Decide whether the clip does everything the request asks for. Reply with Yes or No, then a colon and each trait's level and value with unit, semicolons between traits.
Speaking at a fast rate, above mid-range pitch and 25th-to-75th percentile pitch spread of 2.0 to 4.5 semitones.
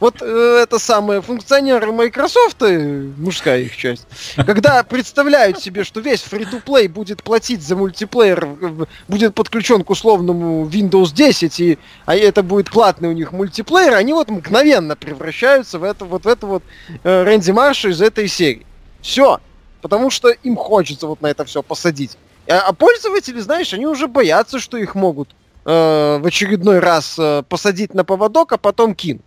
No: fast, 170 wpm; high, 205 Hz; wide, 5.5 semitones